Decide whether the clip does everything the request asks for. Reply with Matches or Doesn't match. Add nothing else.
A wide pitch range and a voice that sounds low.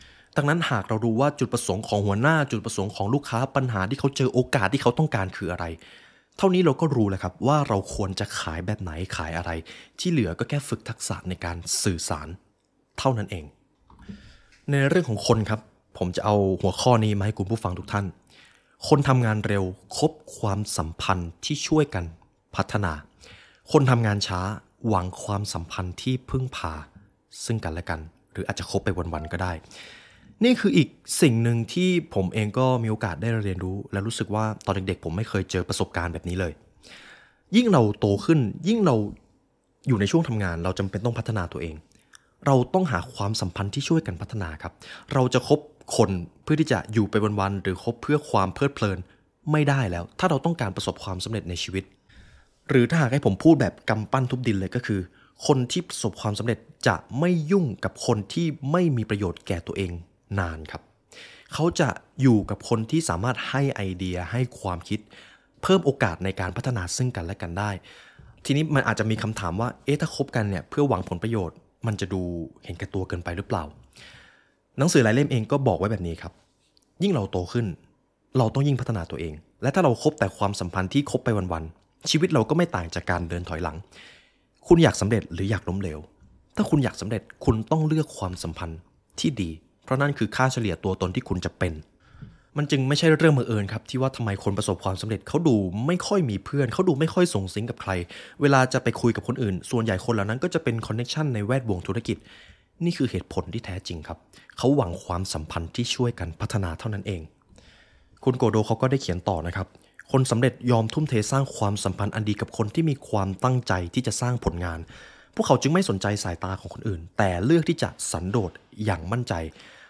Matches